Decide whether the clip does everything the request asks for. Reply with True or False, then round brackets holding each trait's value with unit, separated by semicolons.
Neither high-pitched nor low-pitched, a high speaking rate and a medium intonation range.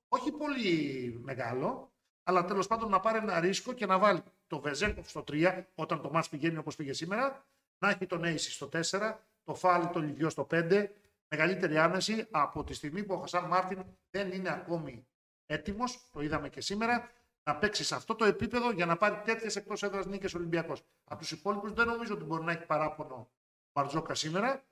True (180 Hz; 190 wpm; 5.0 semitones)